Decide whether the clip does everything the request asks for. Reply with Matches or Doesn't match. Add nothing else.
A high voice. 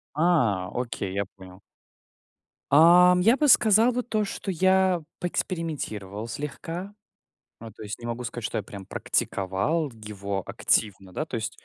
Doesn't match